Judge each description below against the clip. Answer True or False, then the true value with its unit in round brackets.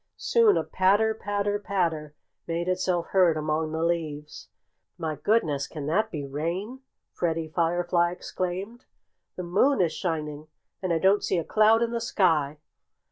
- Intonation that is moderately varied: True (4.2 semitones)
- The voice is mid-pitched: True (175 Hz)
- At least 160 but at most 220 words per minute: False (150 wpm)